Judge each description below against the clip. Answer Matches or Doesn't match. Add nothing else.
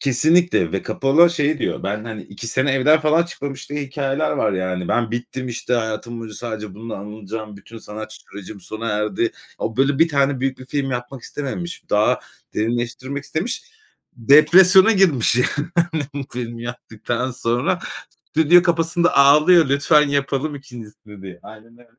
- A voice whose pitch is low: Matches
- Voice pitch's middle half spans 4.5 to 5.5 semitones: Matches